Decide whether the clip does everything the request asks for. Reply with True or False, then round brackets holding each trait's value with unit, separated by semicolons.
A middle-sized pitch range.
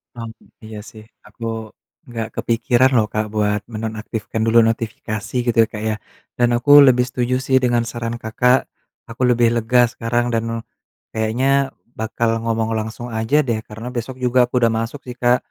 False (1.7 semitones)